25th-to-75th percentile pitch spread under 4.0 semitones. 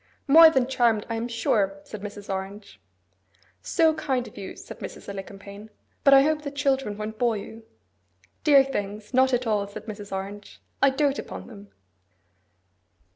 No: average, 4.9 semitones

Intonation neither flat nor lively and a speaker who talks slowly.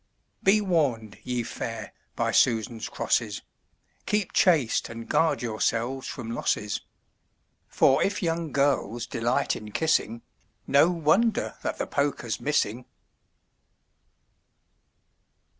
No: wide, 6.0 semitones; slow, 105 wpm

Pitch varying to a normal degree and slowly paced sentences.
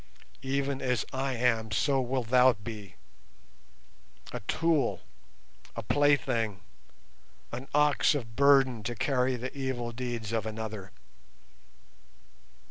Yes: average, 3.2 semitones; slow, 105 wpm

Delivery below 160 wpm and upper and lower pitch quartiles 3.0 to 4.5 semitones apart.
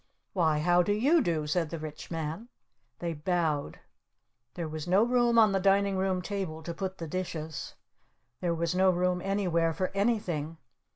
No: average, 170 wpm; average, 3.3 semitones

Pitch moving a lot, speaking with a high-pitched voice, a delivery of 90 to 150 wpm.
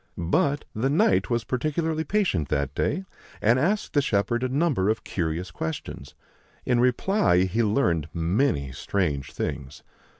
No: wide, 8.9 semitones; low, 110 Hz; average, 140 wpm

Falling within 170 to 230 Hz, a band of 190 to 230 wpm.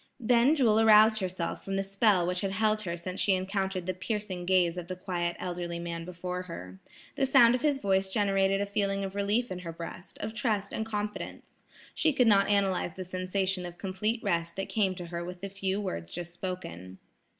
Yes: high, 190 Hz; fast, 205 wpm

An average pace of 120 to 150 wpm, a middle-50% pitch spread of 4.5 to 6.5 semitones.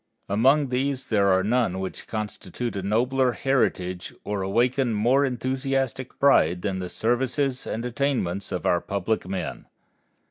Yes: average, 140 wpm; average, 5.2 semitones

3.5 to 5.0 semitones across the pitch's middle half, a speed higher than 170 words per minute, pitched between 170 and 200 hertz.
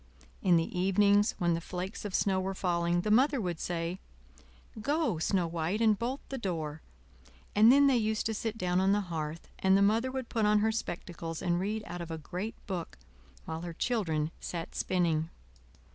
Yes: average, 4.1 semitones; average, 190 wpm; high, 190 Hz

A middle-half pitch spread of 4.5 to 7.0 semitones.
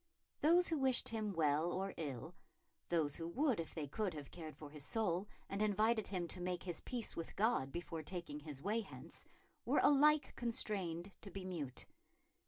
Yes: wide, 5.4 semitones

